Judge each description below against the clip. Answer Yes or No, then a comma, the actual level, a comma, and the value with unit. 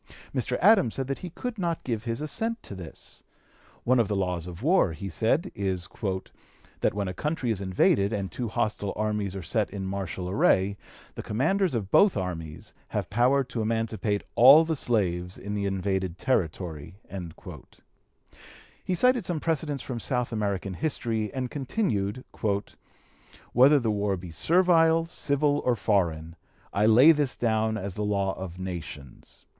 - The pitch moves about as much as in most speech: No, wide, 6.3 semitones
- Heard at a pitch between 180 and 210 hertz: No, low, 110 Hz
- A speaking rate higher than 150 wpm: Yes, average, 160 wpm